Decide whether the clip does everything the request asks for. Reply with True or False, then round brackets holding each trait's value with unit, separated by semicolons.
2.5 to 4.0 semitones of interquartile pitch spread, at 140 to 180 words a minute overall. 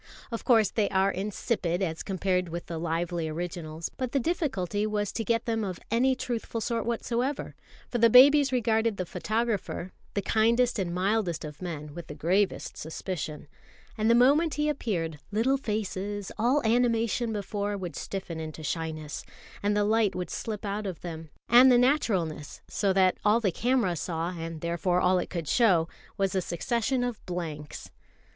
False (5.2 semitones; 170 wpm)